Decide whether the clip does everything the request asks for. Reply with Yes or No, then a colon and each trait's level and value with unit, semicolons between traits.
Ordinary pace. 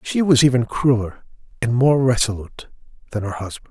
Yes: average, 160 wpm